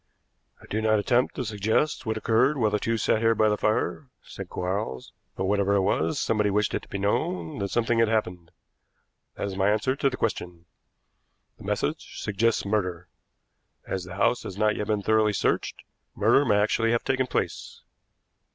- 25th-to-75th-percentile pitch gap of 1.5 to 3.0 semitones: Yes, narrow, 2.5 semitones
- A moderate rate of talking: Yes, average, 190 wpm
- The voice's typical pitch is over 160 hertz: No, low, 105 Hz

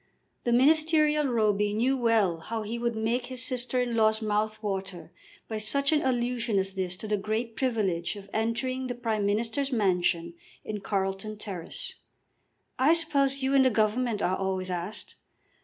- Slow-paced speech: No, average, 165 wpm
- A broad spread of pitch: No, average, 4.0 semitones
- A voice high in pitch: Yes, high, 220 Hz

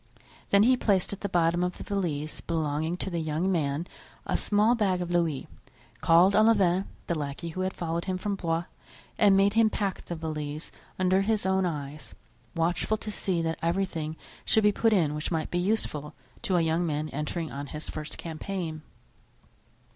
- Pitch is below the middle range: No, medium, 175 Hz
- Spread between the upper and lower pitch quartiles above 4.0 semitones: No, average, 3.7 semitones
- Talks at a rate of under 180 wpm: No, average, 185 wpm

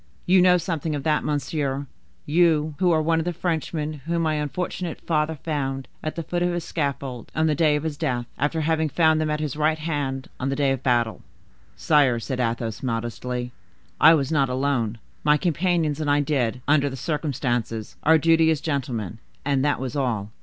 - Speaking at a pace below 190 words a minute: No, average, 195 wpm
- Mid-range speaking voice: Yes, medium, 150 Hz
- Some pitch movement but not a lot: Yes, average, 3.3 semitones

